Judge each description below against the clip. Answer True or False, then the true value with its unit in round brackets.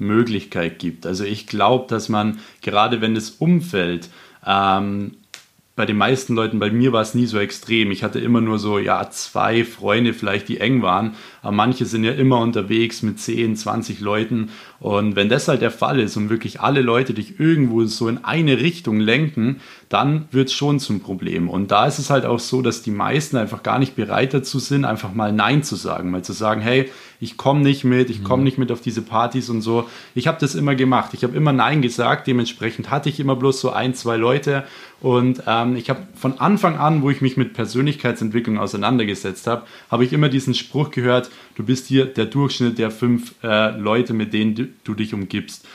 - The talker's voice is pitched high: False (120 Hz)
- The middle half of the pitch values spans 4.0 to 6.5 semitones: False (3.4 semitones)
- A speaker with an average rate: False (210 wpm)